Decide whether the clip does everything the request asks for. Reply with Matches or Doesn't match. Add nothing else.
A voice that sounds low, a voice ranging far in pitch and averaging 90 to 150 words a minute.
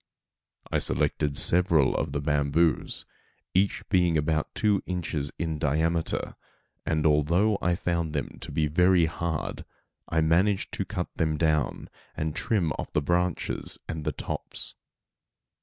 Doesn't match